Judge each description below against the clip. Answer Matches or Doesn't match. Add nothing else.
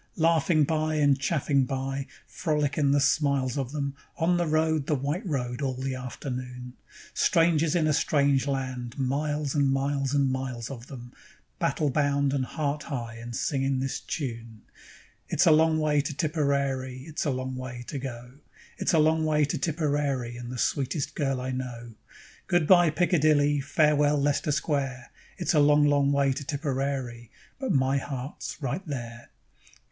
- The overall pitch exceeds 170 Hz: Doesn't match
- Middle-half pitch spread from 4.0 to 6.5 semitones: Doesn't match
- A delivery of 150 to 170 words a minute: Matches